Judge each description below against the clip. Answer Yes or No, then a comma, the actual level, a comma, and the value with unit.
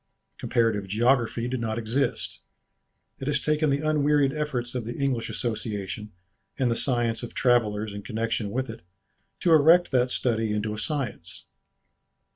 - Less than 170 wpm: Yes, average, 150 wpm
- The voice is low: Yes, low, 120 Hz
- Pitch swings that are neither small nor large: Yes, average, 3.9 semitones